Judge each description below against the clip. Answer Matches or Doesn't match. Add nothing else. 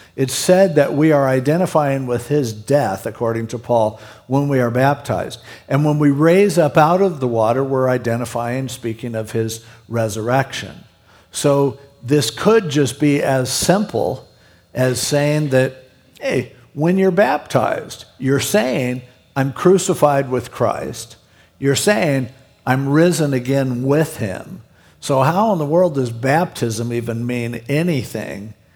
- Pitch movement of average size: Matches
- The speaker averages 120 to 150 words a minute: Matches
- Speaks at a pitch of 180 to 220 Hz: Doesn't match